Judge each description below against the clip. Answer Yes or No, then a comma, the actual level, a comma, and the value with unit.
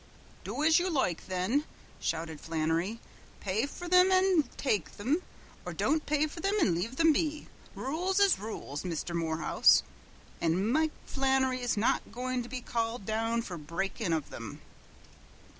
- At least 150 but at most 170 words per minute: Yes, average, 155 wpm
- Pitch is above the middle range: Yes, high, 235 Hz